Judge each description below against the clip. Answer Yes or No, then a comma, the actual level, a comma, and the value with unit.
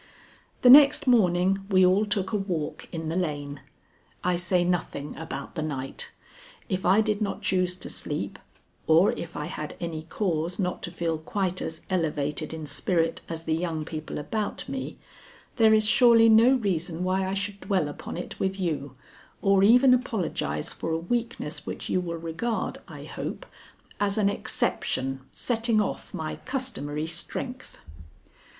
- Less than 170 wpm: Yes, average, 160 wpm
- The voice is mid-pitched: Yes, medium, 180 Hz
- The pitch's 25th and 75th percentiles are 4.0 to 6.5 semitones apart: Yes, average, 4.6 semitones